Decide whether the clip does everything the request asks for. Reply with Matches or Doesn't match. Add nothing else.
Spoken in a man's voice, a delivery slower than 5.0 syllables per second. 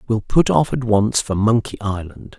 Matches